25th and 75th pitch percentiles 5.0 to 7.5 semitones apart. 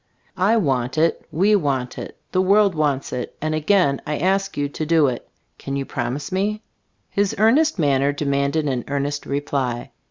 Yes: wide, 5.4 semitones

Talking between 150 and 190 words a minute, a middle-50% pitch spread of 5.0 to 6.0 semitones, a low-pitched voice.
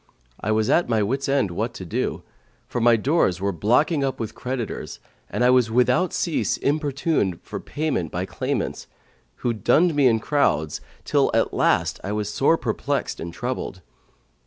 Yes: average, 170 wpm; average, 5.3 semitones; low, 120 Hz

